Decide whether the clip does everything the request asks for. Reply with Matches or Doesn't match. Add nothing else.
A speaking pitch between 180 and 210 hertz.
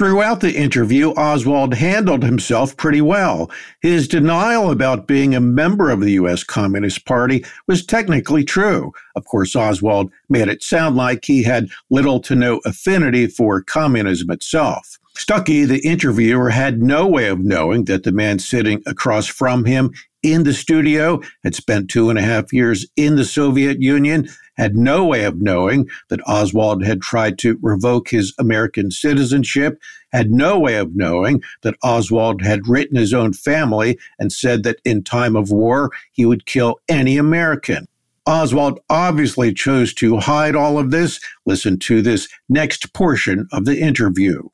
Doesn't match